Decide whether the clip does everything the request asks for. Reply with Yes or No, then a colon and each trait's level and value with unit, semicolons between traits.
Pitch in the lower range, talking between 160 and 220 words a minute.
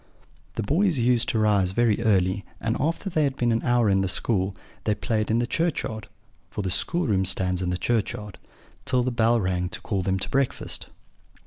Yes: low, 110 Hz; average, 195 wpm